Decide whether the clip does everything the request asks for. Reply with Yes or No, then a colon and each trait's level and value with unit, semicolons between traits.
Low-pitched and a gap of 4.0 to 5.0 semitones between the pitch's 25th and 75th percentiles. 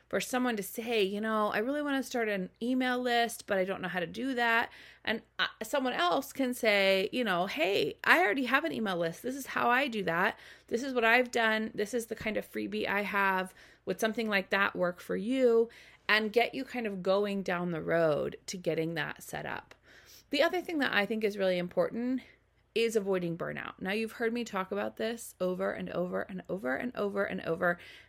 No: high, 215 Hz; average, 4.3 semitones